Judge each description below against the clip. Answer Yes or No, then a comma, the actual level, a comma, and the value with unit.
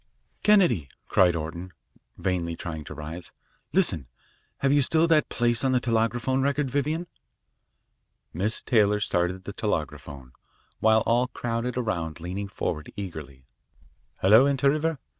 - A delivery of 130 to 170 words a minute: Yes, slow, 135 wpm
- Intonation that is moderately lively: No, wide, 7.6 semitones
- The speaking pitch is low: Yes, low, 110 Hz